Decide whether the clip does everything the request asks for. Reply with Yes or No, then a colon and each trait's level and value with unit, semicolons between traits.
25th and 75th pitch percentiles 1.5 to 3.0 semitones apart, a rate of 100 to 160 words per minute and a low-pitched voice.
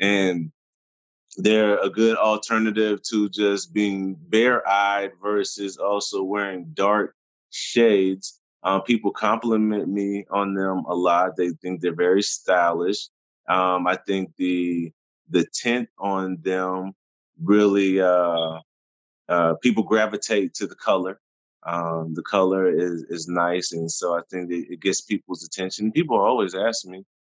Yes: average, 2.7 semitones; slow, 135 wpm; very low, 95 Hz